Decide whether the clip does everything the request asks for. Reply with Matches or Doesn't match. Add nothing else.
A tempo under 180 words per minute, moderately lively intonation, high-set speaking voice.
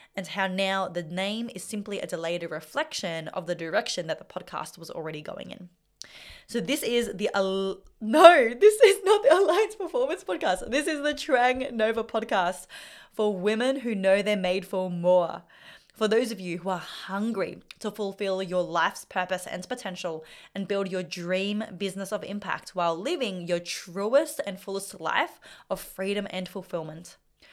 Matches